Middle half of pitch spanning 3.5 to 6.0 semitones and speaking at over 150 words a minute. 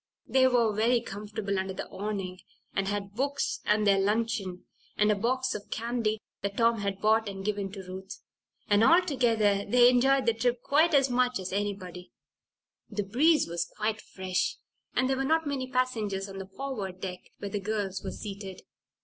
Yes: average, 4.0 semitones; average, 180 wpm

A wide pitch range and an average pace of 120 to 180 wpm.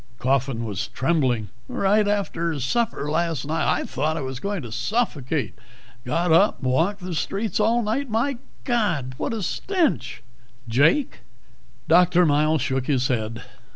Yes: wide, 7.7 semitones; average, 150 wpm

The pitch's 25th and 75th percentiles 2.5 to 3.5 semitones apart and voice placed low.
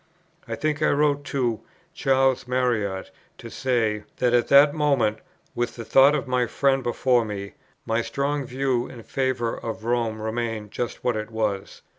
Yes: average, 3.1 semitones; low, 120 Hz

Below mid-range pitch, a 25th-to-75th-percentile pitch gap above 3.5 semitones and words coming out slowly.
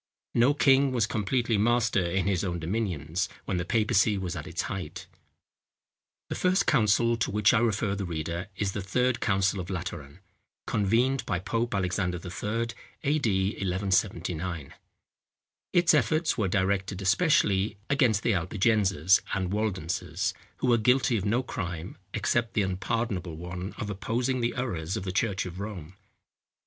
No: low, 100 Hz; average, 4.2 semitones; average, 150 wpm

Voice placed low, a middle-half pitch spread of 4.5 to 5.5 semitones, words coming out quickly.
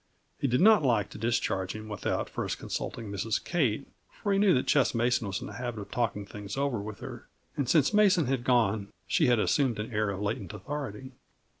Yes: low, 120 Hz; average, 4.9 semitones; fast, 210 wpm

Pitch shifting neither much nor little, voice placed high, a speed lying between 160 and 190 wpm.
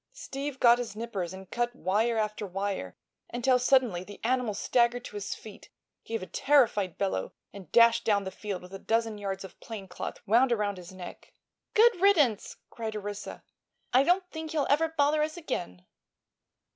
Yes: average, 4.8 semitones; high, 225 Hz; average, 175 wpm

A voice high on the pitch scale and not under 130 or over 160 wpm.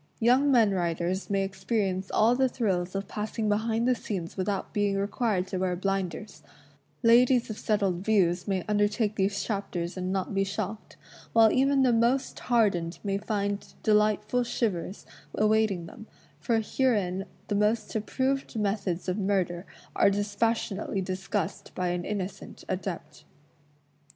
Yes: high, 205 Hz; average, 150 wpm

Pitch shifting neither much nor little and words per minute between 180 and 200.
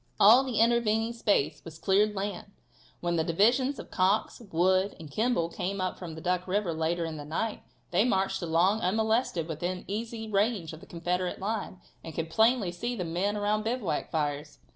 Yes: average, 4.6 semitones; average, 185 wpm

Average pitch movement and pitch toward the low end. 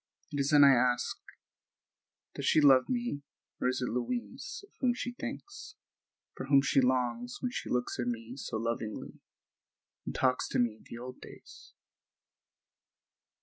Yes: average, 4.5 semitones; low, 130 Hz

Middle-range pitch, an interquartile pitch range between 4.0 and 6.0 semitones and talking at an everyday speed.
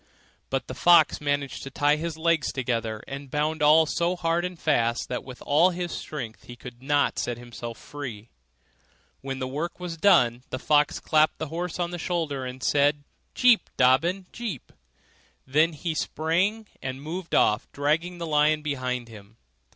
Yes: medium, 150 Hz; average, 4.4 semitones; average, 175 wpm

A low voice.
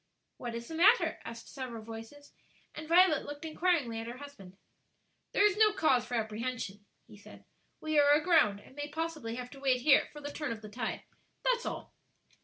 No: very high, 275 Hz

